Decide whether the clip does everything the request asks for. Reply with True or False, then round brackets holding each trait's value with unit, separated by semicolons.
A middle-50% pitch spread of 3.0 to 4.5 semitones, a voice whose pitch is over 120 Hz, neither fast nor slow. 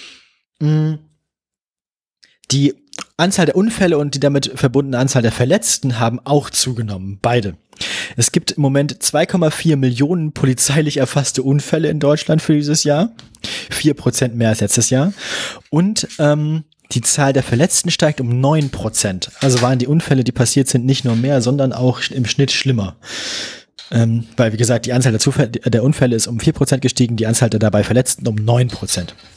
True (3.8 semitones; 135 Hz; 160 wpm)